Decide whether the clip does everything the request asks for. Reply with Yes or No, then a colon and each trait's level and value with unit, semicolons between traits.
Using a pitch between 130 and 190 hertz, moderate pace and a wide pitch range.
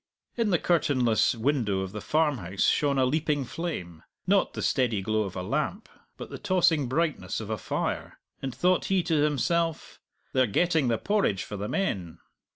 Yes: low, 135 Hz; average, 175 wpm; wide, 7.4 semitones